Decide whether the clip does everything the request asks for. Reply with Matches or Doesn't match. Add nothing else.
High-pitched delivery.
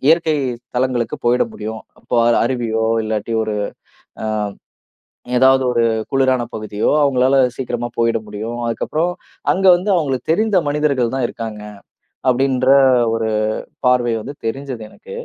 Doesn't match